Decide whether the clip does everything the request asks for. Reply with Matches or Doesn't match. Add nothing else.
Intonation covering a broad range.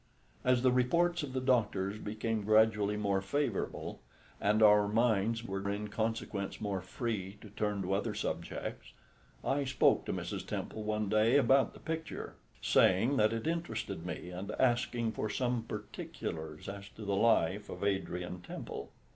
Doesn't match